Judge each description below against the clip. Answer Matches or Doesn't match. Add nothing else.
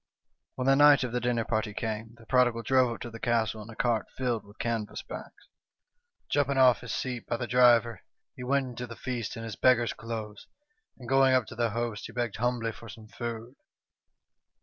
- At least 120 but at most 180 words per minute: Doesn't match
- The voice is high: Doesn't match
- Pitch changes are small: Matches